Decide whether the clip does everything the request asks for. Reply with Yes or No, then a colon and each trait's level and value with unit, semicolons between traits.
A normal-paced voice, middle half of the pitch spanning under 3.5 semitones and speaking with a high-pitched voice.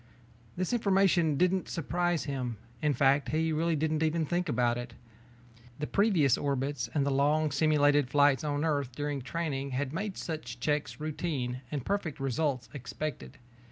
No: average, 155 wpm; average, 3.0 semitones; medium, 145 Hz